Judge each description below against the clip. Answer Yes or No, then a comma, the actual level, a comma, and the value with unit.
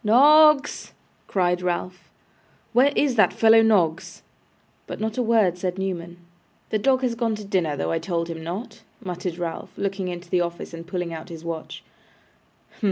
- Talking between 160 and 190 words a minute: Yes, average, 175 wpm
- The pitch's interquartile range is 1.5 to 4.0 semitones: No, average, 4.5 semitones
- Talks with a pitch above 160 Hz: Yes, medium, 185 Hz